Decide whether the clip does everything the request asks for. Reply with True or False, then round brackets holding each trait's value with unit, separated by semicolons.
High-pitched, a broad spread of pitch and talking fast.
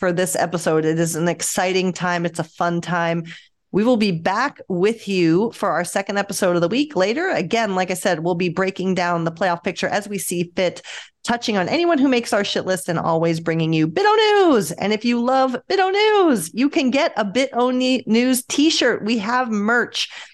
True (195 Hz; 6.0 semitones; 210 wpm)